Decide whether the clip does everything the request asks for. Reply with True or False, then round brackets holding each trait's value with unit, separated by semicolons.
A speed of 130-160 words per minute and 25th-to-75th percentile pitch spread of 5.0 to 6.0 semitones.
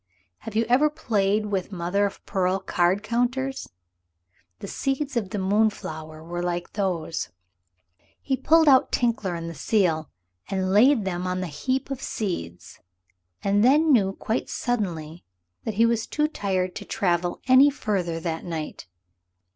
True (150 wpm; 5.6 semitones)